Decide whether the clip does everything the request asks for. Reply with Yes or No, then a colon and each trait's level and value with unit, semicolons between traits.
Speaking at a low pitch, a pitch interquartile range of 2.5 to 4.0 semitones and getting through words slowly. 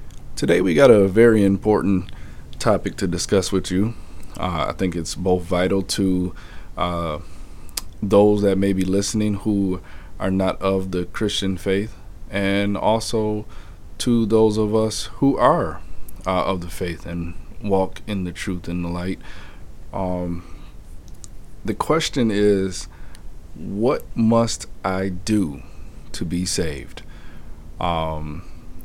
Yes: very low, 95 Hz; average, 2.9 semitones; slow, 130 wpm